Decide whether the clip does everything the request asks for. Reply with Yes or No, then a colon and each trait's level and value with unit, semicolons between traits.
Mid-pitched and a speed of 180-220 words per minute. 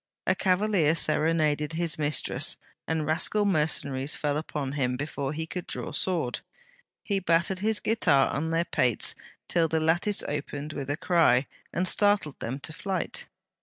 No: medium, 160 Hz; average, 155 wpm